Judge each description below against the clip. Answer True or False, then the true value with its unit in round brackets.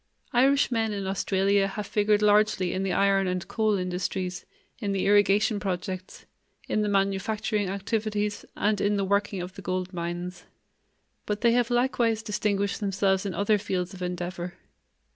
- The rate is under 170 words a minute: True (155 wpm)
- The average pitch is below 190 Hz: False (200 Hz)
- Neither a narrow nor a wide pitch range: False (2.1 semitones)